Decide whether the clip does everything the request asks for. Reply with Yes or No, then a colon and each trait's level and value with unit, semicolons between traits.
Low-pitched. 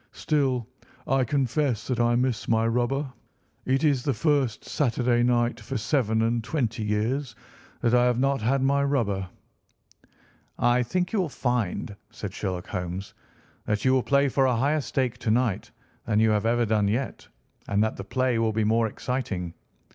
Yes: low, 120 Hz